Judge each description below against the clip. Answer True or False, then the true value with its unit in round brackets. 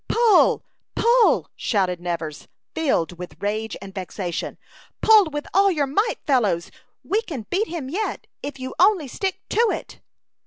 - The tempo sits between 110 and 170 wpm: True (150 wpm)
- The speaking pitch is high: True (285 Hz)